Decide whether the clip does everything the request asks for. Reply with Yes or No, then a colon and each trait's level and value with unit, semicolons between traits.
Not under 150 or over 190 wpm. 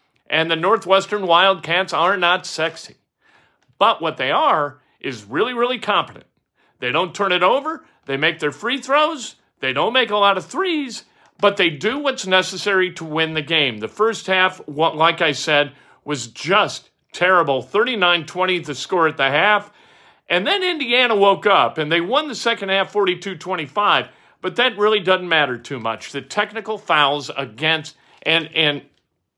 Yes: average, 170 wpm